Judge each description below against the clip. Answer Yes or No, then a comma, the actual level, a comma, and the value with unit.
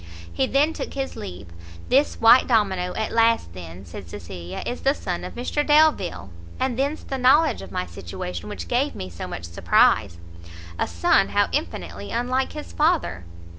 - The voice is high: Yes, high, 205 Hz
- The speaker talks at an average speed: Yes, average, 170 wpm